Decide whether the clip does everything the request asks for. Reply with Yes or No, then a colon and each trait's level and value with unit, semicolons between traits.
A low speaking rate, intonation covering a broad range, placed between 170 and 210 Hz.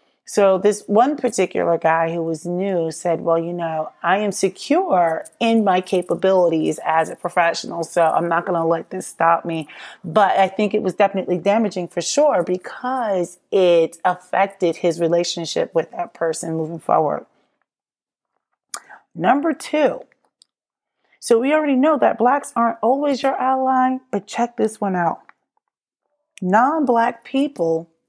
No: average, 145 wpm; wide, 6.0 semitones; high, 190 Hz